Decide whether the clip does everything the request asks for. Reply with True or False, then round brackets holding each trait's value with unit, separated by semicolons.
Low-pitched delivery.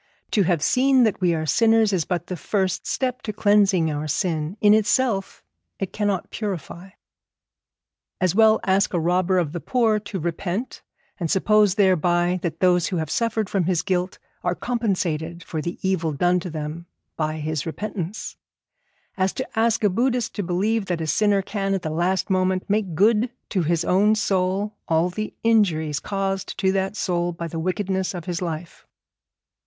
False (185 Hz)